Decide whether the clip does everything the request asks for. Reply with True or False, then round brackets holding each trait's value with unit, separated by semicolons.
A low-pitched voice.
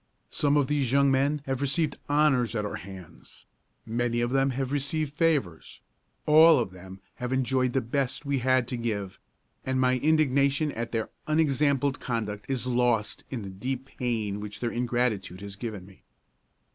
True (125 Hz)